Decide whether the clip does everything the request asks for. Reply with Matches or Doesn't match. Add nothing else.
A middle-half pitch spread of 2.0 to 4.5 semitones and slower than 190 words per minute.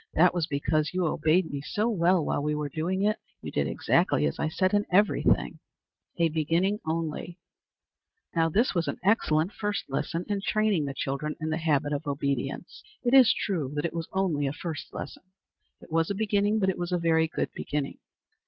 Doesn't match